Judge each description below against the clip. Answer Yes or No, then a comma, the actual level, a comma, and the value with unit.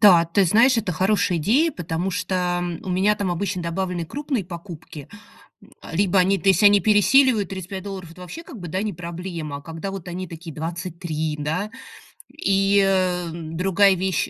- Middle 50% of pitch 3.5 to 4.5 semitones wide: No, average, 2.9 semitones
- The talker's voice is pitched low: No, medium, 185 Hz